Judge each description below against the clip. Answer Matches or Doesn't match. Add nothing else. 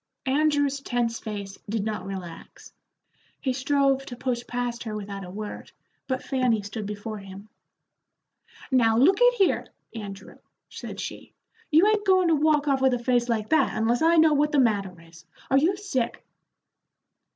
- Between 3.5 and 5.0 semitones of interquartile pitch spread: Doesn't match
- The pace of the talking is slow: Doesn't match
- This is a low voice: Doesn't match